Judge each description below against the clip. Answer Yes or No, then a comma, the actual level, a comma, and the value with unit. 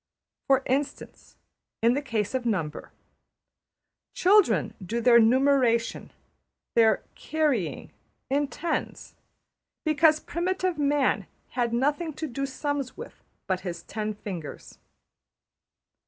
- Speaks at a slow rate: Yes, slow, 105 wpm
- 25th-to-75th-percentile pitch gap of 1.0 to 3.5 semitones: No, average, 4.6 semitones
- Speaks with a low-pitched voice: No, very high, 260 Hz